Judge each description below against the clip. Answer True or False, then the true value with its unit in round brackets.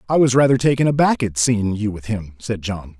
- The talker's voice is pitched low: True (115 Hz)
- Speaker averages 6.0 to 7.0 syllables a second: False (5.4 syllables/s)